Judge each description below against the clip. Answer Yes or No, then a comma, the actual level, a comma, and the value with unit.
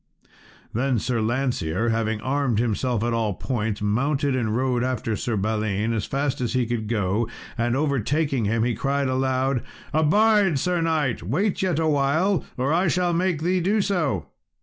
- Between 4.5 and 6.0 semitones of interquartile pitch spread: Yes, average, 5.2 semitones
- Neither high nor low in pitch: No, low, 130 Hz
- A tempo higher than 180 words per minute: No, average, 165 wpm